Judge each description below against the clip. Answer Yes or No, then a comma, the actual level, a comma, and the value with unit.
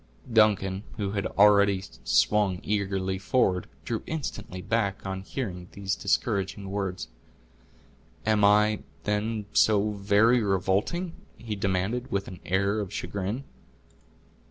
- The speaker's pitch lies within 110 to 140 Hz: No, low, 100 Hz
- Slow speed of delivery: Yes, slow, 115 wpm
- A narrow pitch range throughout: Yes, narrow, 1.9 semitones